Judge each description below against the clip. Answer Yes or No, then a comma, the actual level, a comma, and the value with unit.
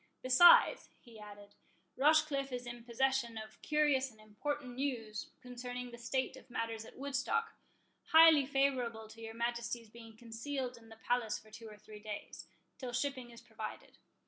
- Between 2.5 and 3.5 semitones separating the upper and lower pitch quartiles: Yes, average, 3.1 semitones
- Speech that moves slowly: No, average, 160 wpm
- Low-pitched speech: No, high, 240 Hz